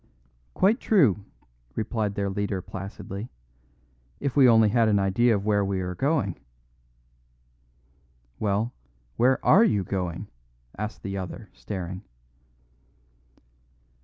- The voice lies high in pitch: No, low, 105 Hz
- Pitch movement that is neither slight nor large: Yes, average, 3.2 semitones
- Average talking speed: No, slow, 110 wpm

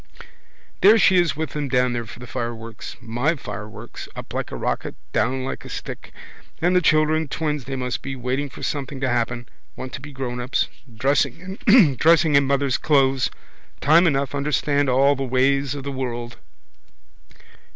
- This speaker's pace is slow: No, average, 165 wpm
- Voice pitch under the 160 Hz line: Yes, low, 135 Hz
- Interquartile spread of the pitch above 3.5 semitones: No, average, 2.9 semitones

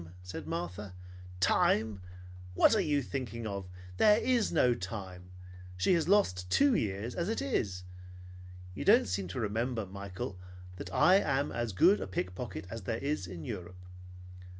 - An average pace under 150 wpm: No, average, 155 wpm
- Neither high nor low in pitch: No, low, 105 Hz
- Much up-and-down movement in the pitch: Yes, wide, 7.2 semitones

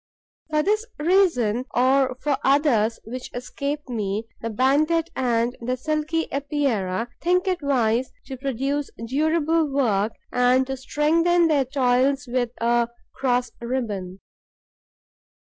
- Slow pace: Yes, slow, 120 wpm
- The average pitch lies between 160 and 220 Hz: No, very high, 265 Hz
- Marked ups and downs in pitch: No, average, 3.9 semitones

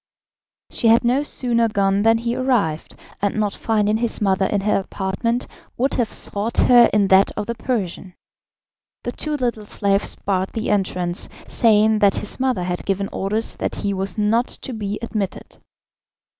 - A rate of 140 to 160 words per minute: No, average, 170 wpm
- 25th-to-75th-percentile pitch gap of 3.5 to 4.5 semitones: No, average, 3.0 semitones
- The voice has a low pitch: No, high, 210 Hz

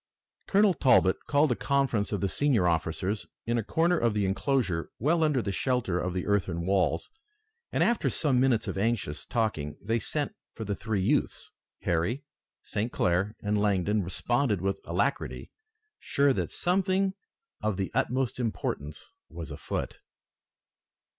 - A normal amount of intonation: No, wide, 6.1 semitones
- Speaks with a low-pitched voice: Yes, low, 110 Hz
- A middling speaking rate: Yes, average, 150 wpm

